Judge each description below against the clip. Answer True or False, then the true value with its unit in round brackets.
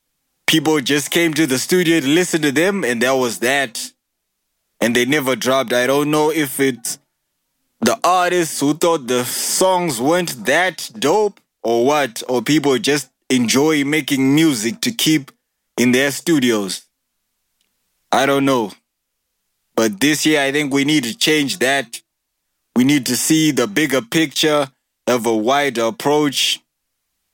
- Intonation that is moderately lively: True (3.8 semitones)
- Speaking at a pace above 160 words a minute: False (150 wpm)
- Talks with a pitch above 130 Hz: True (140 Hz)